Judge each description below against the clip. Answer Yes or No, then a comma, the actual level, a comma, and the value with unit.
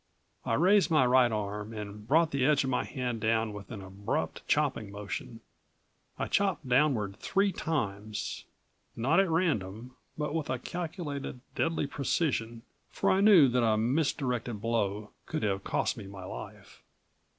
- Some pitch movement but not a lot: No, wide, 6.3 semitones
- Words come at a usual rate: Yes, average, 155 wpm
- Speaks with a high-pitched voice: No, low, 125 Hz